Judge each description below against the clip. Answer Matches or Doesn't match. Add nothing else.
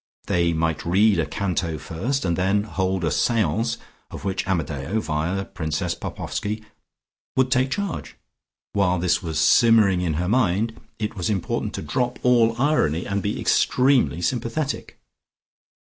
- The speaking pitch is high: Doesn't match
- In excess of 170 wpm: Doesn't match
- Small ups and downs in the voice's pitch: Doesn't match